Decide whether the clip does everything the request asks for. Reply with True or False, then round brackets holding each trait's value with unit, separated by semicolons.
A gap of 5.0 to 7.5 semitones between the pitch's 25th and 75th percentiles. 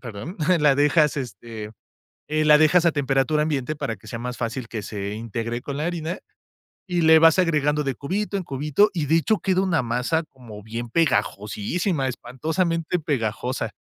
True (5.5 semitones)